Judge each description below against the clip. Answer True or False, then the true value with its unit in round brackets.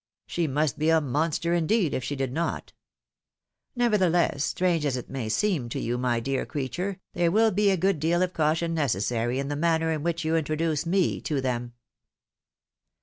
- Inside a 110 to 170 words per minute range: False (185 wpm)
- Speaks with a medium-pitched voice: True (160 Hz)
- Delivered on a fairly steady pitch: False (4.2 semitones)